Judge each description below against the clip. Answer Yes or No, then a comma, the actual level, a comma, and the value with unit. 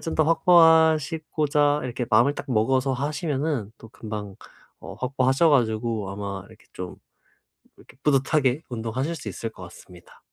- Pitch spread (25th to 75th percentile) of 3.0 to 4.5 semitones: No, average, 5.3 semitones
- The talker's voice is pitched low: Yes, low, 130 Hz